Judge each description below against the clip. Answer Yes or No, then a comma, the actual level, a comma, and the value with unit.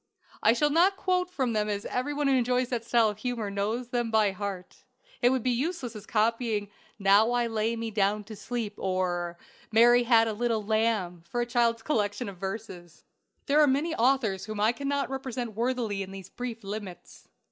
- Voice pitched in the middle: No, high, 225 Hz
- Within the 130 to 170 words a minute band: No, average, 200 wpm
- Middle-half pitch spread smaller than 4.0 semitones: Yes, average, 3.3 semitones